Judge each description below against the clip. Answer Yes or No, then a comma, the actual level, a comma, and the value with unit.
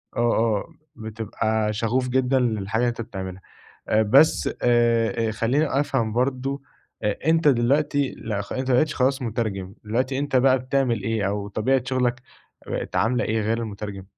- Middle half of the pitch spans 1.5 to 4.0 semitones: Yes, average, 3.1 semitones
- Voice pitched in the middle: No, low, 115 Hz